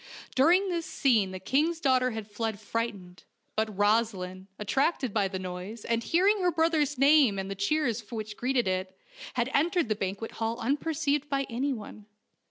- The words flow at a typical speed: Yes, average, 165 wpm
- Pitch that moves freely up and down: Yes, wide, 5.9 semitones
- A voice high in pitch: Yes, high, 230 Hz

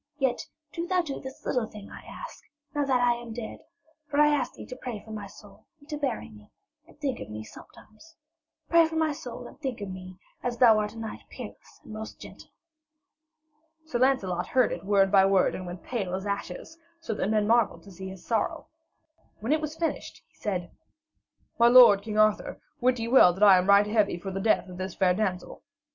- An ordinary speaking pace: No, fast, 215 wpm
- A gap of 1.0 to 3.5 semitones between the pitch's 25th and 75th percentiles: No, average, 5.2 semitones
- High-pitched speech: Yes, high, 220 Hz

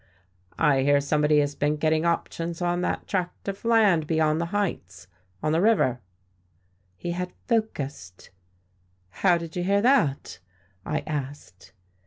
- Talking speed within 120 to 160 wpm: Yes, average, 140 wpm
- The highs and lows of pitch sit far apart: No, average, 4.0 semitones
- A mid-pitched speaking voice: Yes, medium, 160 Hz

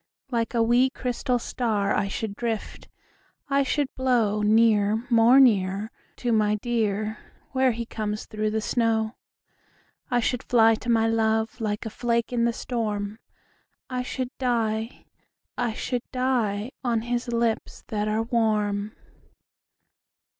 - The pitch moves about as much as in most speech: No, narrow, 2.2 semitones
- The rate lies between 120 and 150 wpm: Yes, average, 140 wpm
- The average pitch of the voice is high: Yes, high, 225 Hz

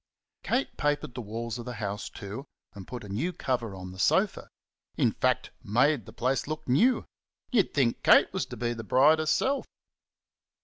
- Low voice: Yes, low, 125 Hz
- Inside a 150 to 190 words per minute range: Yes, average, 180 wpm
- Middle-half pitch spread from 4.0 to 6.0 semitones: Yes, wide, 5.5 semitones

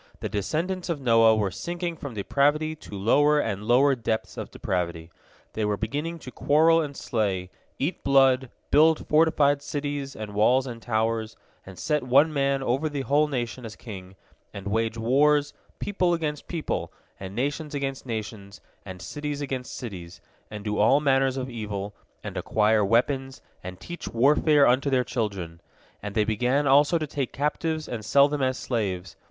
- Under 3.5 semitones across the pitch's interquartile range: No, average, 5.3 semitones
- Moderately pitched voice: No, low, 130 Hz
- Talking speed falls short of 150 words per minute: No, average, 170 wpm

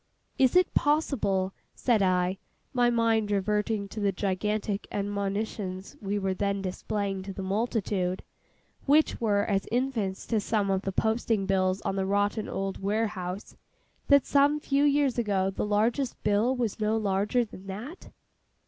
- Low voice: No, high, 205 Hz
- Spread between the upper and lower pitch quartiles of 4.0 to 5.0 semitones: No, average, 3.0 semitones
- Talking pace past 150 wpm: No, average, 145 wpm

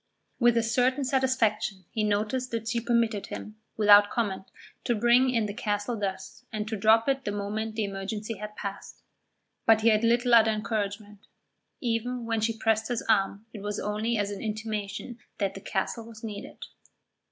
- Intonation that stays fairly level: Yes, narrow, 2.1 semitones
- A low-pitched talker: No, high, 220 Hz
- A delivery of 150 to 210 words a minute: Yes, average, 175 wpm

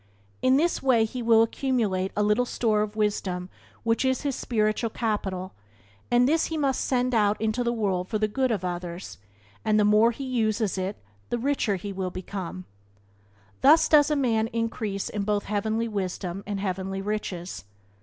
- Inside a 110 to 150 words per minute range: No, average, 175 wpm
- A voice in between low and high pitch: No, high, 215 Hz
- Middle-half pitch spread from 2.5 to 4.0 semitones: Yes, average, 3.7 semitones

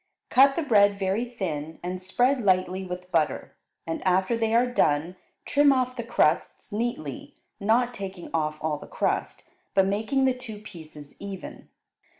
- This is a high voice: Yes, high, 195 Hz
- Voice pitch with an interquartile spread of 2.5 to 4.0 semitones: No, average, 5.2 semitones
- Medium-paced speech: Yes, average, 155 wpm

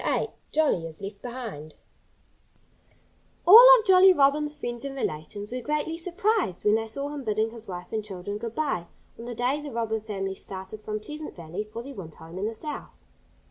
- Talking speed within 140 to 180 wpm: No, average, 190 wpm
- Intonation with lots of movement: Yes, wide, 6.7 semitones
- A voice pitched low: No, high, 225 Hz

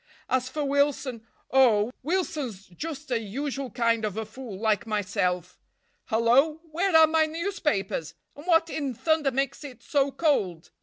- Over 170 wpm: No, average, 140 wpm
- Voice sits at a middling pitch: No, very high, 265 Hz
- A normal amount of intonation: No, wide, 5.7 semitones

